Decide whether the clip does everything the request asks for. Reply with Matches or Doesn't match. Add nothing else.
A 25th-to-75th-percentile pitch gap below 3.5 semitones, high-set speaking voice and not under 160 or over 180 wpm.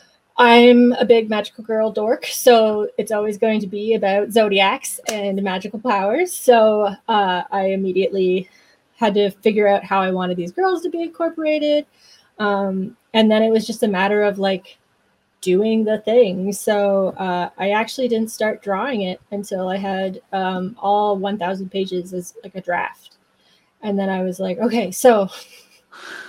Matches